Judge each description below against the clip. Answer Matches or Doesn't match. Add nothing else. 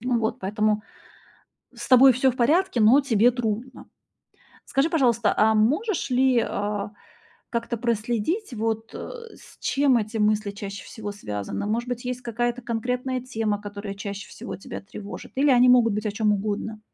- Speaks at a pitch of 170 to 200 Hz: Doesn't match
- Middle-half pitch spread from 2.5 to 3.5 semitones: Matches